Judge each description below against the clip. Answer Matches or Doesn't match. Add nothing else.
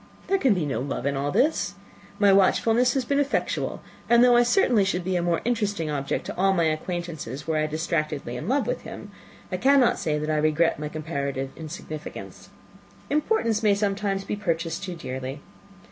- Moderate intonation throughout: Doesn't match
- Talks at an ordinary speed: Matches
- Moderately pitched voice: Matches